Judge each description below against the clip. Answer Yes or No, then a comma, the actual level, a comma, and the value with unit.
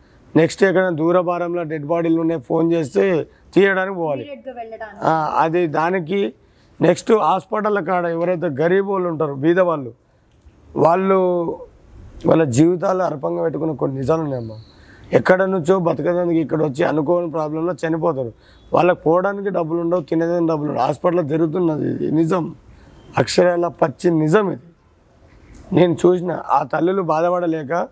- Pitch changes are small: Yes, narrow, 2.3 semitones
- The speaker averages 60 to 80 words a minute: No, average, 120 wpm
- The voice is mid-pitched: Yes, medium, 170 Hz